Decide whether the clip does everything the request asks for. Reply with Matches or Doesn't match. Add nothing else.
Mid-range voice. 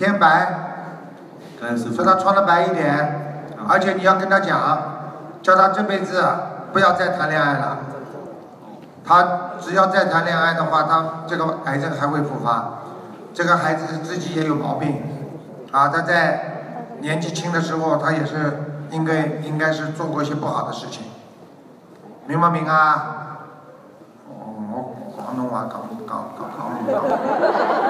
Matches